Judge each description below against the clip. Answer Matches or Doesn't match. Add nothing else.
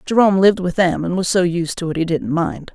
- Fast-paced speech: Matches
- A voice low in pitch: Doesn't match